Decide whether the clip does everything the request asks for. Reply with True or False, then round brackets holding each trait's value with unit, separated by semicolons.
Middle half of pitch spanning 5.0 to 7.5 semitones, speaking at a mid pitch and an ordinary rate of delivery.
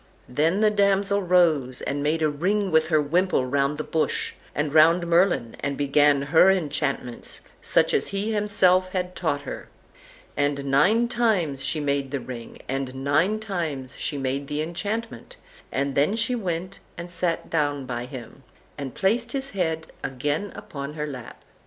True (5.3 semitones; 155 Hz; 165 wpm)